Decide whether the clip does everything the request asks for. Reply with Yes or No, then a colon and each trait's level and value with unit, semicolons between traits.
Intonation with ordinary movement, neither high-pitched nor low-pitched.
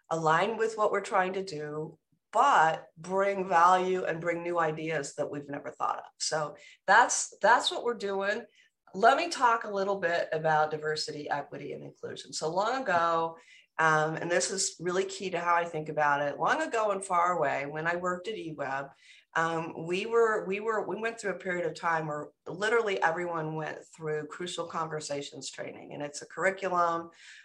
Yes: average, 3.9 semitones; medium, 170 Hz